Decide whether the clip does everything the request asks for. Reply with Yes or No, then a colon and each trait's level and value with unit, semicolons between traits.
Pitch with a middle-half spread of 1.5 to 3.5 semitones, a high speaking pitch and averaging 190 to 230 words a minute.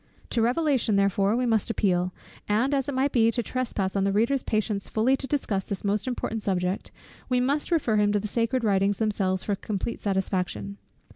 No: average, 4.0 semitones; high, 215 Hz; average, 195 wpm